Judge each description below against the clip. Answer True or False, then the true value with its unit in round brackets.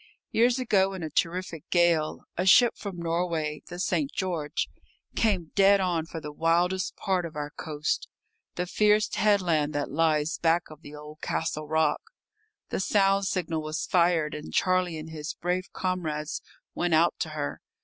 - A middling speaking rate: True (165 wpm)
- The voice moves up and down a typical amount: True (3.2 semitones)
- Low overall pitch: False (170 Hz)